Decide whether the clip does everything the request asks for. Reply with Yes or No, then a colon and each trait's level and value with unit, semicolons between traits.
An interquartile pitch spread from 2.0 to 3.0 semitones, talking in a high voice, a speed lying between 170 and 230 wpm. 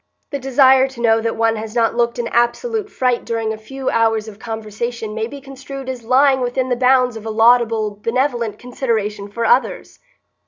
Yes: average, 2.7 semitones; high, 235 Hz; average, 190 wpm